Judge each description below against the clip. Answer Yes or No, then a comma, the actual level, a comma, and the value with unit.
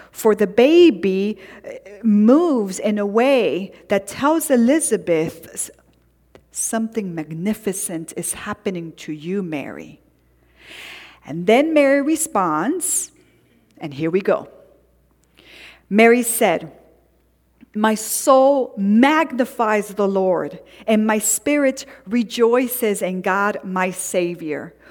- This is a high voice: Yes, high, 215 Hz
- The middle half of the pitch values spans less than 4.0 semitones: No, average, 5.1 semitones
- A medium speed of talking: No, slow, 95 wpm